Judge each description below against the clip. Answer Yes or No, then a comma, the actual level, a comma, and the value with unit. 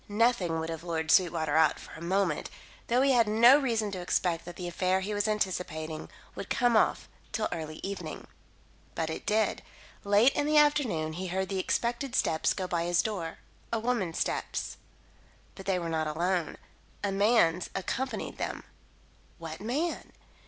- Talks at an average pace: Yes, average, 170 wpm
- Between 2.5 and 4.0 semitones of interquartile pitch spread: No, average, 5.2 semitones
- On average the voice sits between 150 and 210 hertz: Yes, high, 190 Hz